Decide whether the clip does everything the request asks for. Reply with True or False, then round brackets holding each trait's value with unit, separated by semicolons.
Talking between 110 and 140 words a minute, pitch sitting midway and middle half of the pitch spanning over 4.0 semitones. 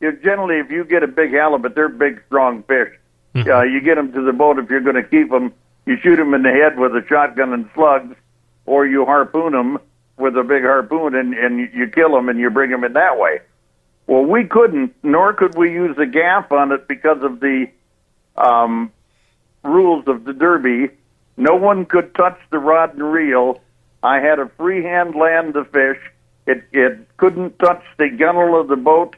False (205 wpm; 145 Hz; 4.6 semitones)